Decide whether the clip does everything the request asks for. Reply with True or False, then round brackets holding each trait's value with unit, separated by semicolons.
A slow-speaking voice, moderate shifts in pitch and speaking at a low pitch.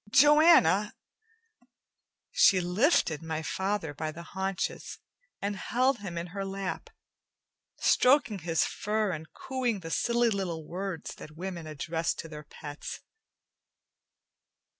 False (120 wpm; 4.6 semitones; 190 Hz)